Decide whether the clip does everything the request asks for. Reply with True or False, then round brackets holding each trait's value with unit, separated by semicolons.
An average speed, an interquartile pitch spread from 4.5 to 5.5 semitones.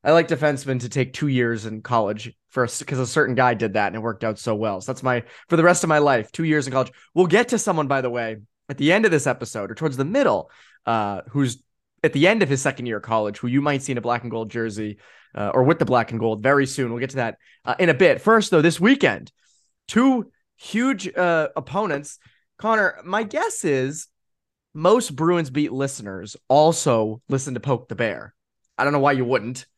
False (240 wpm; 5.0 semitones)